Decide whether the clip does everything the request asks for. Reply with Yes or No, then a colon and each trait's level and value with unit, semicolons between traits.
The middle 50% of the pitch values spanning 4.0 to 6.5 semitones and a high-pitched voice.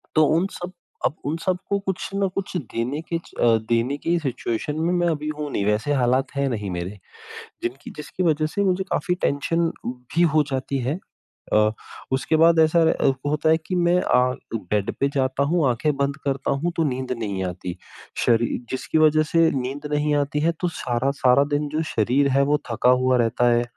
No: average, 4.5 semitones; medium, 140 Hz